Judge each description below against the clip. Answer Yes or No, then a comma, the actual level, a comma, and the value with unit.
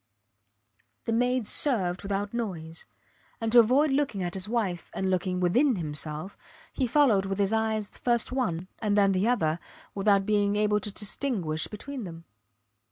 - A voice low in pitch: No, high, 205 Hz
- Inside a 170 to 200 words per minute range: No, average, 160 wpm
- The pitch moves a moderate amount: Yes, average, 4.3 semitones